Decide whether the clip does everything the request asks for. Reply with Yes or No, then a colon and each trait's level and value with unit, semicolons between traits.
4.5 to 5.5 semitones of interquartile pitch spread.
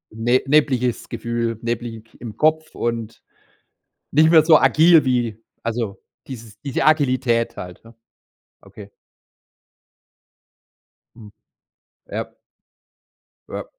No: average, 3.8 semitones